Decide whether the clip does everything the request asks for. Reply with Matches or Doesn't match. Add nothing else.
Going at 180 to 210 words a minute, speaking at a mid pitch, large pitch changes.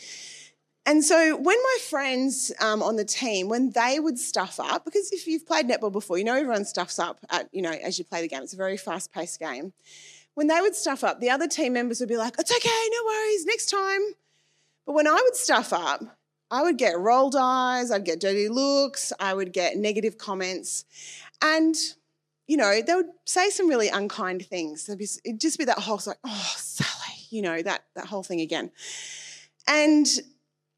Doesn't match